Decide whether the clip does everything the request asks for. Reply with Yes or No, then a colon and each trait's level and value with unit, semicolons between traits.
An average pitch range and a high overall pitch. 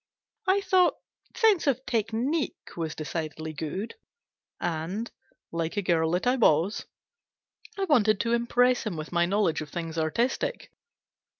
No: wide, 7.4 semitones; high, 205 Hz